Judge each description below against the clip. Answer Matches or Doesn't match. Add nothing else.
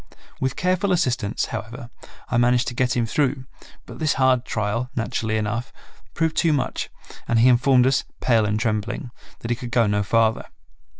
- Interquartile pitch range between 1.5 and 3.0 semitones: Matches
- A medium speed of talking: Matches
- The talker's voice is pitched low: Matches